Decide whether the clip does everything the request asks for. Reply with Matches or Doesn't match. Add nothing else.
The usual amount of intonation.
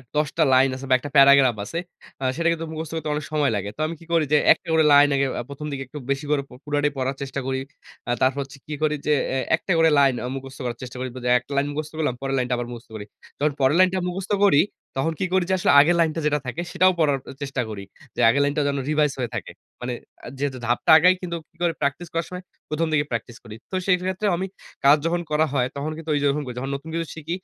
Matches